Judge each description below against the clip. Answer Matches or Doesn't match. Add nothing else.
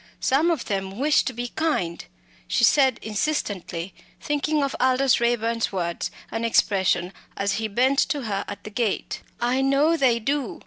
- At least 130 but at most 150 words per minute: Doesn't match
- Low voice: Doesn't match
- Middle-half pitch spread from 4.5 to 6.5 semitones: Matches